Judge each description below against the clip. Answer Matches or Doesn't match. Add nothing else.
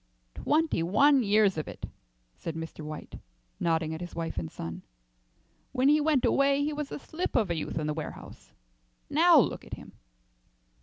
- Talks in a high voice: Matches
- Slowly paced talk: Doesn't match